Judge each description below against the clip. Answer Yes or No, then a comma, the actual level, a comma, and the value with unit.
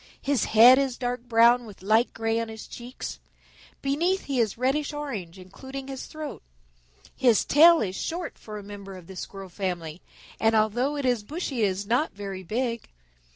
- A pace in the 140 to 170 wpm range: No, average, 180 wpm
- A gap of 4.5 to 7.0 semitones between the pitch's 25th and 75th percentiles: Yes, average, 5.0 semitones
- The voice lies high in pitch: Yes, high, 235 Hz